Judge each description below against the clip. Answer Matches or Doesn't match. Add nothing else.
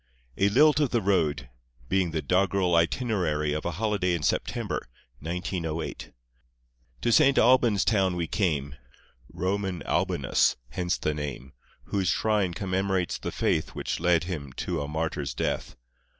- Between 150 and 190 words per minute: Doesn't match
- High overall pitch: Doesn't match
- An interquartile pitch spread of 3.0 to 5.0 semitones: Matches